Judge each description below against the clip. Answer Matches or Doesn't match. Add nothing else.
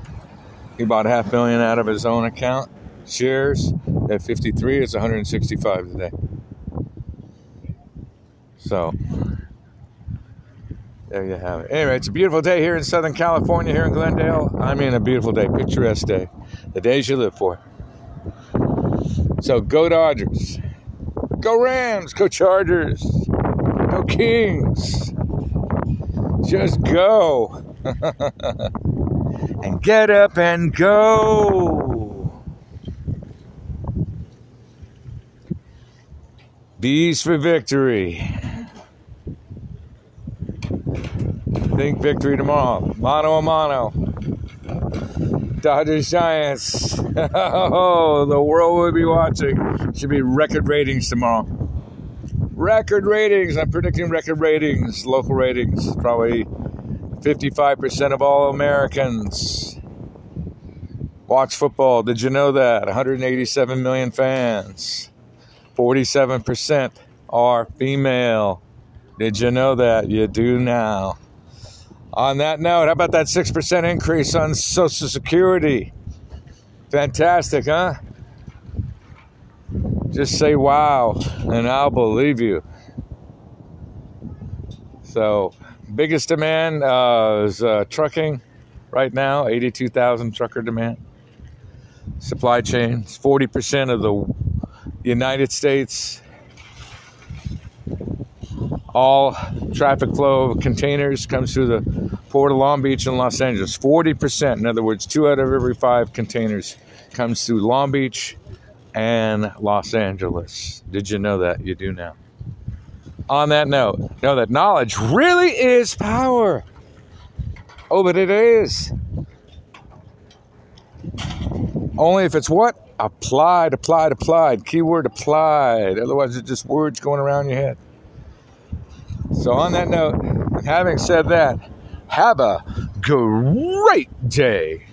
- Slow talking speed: Matches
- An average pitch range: Matches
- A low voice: Matches